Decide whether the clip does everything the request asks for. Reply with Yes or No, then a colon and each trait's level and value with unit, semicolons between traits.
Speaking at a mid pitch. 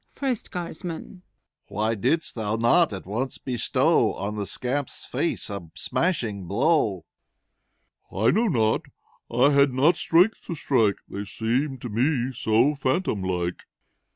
No: low, 125 Hz